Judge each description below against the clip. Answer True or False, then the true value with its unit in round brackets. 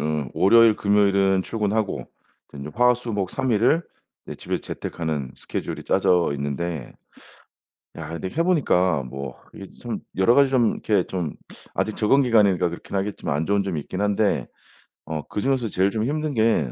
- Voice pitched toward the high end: False (100 Hz)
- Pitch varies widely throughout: True (5.7 semitones)